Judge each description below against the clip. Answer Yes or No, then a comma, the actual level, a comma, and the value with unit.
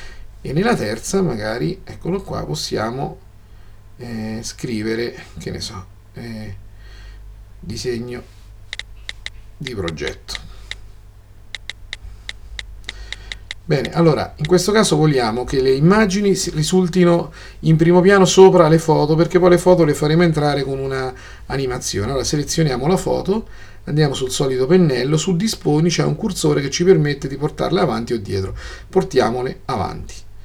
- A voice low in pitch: Yes, low, 125 Hz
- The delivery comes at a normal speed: Yes, average, 130 wpm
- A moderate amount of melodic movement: No, wide, 8.3 semitones